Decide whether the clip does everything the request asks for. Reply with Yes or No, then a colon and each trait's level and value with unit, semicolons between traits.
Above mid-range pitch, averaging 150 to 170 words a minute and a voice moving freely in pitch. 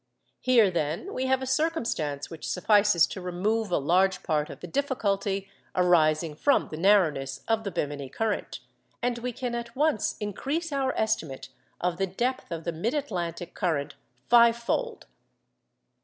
Yes: high, 200 Hz; average, 155 wpm; wide, 6.4 semitones